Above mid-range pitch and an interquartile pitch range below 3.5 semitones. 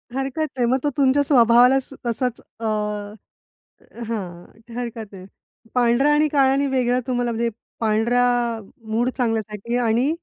Yes: high, 245 Hz; average, 2.7 semitones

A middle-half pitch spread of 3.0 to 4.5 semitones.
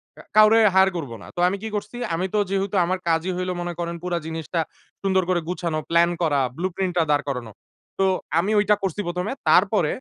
No: narrow, 2.4 semitones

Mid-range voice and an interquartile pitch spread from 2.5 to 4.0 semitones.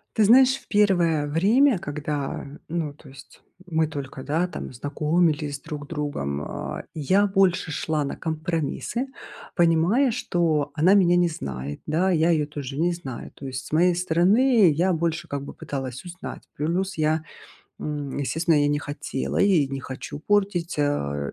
Yes: medium, 160 Hz; average, 3.7 semitones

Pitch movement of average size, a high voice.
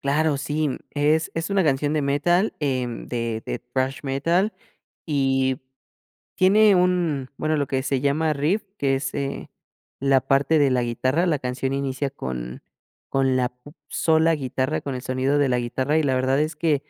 No: average, 3.0 semitones; medium, 140 Hz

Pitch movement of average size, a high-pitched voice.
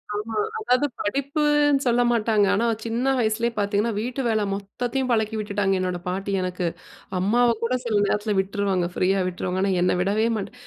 Yes: average, 3.5 semitones; high, 215 Hz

